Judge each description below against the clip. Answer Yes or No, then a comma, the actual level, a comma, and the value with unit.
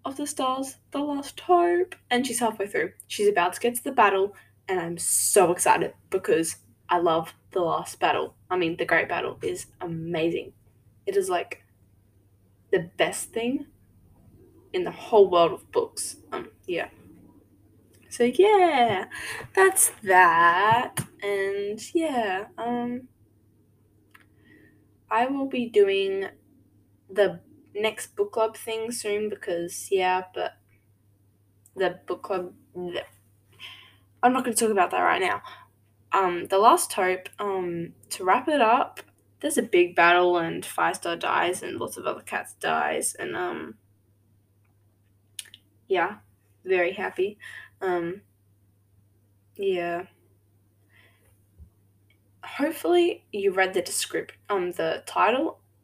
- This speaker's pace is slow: Yes, slow, 130 wpm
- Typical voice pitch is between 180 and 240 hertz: Yes, medium, 185 Hz